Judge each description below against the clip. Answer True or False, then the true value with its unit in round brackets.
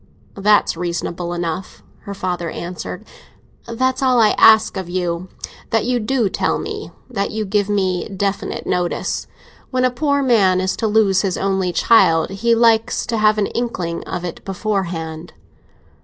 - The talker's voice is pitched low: False (195 Hz)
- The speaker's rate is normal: True (155 wpm)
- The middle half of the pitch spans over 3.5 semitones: True (3.9 semitones)